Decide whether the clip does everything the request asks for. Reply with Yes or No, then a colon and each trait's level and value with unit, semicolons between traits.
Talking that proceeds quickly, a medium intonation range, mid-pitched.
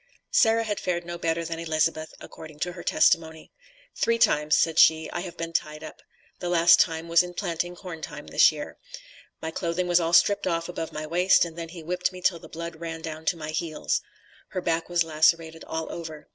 No: fast, 215 wpm; narrow, 1.6 semitones; medium, 165 Hz